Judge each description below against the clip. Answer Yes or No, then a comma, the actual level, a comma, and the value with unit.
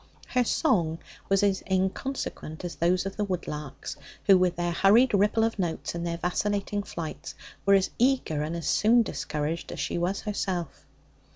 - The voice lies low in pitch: No, medium, 185 Hz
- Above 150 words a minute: Yes, average, 170 wpm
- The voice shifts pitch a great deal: No, average, 3.5 semitones